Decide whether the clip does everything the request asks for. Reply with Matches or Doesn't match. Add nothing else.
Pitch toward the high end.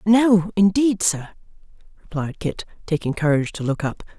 Doesn't match